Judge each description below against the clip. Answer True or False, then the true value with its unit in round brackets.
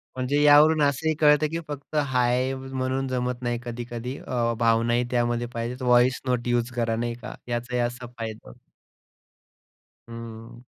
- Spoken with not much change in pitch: True (1.9 semitones)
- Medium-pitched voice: False (125 Hz)